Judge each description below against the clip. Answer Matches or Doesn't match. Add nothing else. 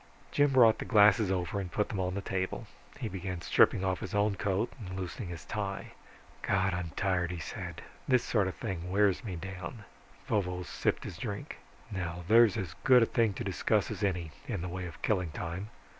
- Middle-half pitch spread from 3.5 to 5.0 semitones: Doesn't match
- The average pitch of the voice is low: Matches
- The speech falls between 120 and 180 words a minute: Doesn't match